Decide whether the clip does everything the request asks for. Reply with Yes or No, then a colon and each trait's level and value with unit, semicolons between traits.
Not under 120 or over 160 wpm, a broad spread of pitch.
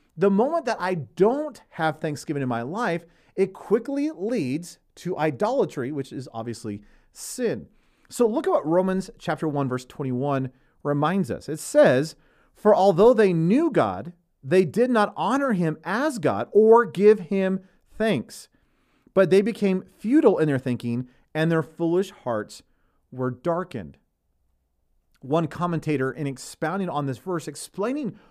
Yes: average, 145 wpm; wide, 6.4 semitones